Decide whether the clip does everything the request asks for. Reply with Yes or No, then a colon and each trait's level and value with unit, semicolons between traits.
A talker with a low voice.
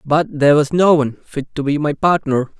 No: medium, 150 Hz